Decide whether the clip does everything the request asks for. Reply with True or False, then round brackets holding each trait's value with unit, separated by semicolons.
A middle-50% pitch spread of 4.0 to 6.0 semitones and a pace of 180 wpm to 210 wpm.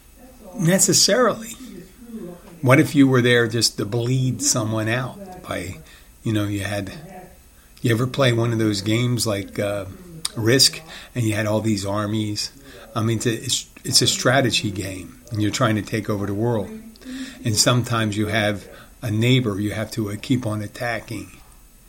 False (4.5 semitones; 165 wpm)